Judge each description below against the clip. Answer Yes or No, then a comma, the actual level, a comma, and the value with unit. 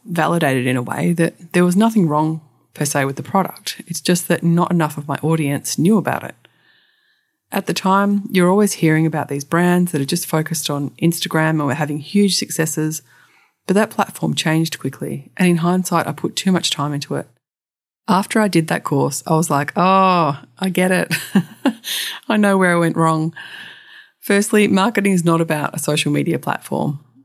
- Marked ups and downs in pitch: No, average, 4.2 semitones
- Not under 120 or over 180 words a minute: No, average, 190 wpm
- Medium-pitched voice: Yes, medium, 165 Hz